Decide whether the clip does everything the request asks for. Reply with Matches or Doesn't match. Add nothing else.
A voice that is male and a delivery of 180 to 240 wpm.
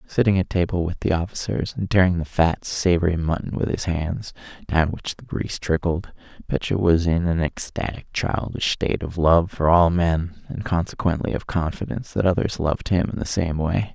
Matches